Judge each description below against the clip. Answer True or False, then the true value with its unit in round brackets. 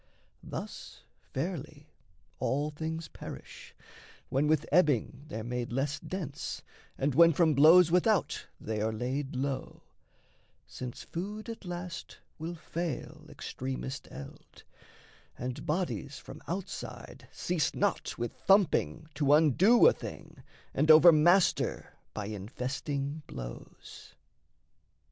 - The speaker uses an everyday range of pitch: True (4.7 semitones)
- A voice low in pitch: False (150 Hz)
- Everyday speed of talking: False (110 wpm)